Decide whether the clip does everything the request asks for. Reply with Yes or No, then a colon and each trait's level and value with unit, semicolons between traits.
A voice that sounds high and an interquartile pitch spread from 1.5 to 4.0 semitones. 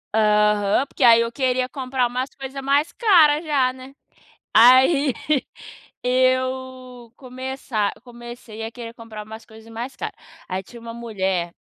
Yes: very high, 250 Hz; narrow, 2.6 semitones